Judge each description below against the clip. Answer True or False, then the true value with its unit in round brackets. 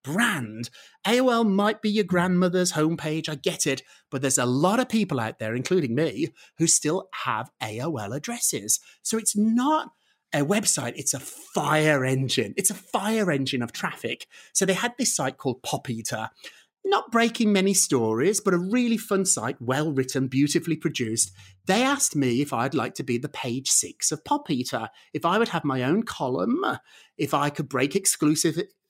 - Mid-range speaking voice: True (160 Hz)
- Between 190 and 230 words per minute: False (180 wpm)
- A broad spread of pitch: True (7.9 semitones)